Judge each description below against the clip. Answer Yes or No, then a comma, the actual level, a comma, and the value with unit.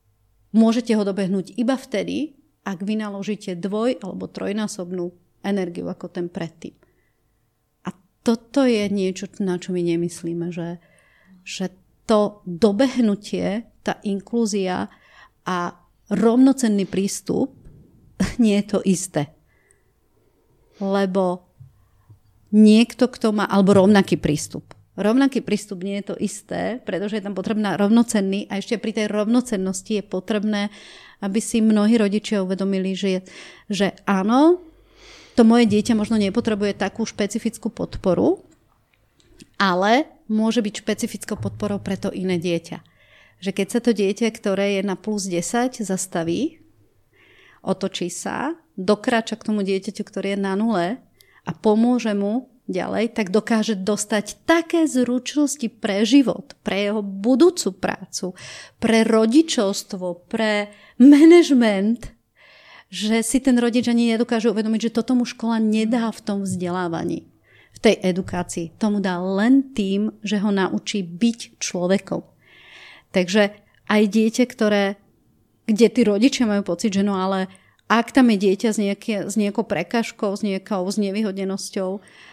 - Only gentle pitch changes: No, average, 3.1 semitones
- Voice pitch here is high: Yes, high, 205 Hz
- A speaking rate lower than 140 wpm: Yes, average, 130 wpm